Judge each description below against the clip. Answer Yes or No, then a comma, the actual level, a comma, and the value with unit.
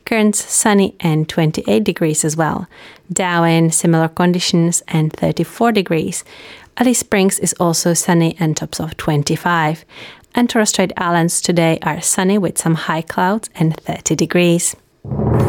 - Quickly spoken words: No, slow, 135 wpm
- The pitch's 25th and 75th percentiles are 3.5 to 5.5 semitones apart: No, average, 2.9 semitones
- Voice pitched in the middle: Yes, medium, 170 Hz